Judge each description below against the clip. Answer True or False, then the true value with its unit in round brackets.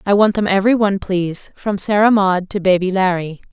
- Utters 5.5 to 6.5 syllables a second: True (5.8 syllables/s)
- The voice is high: True (195 Hz)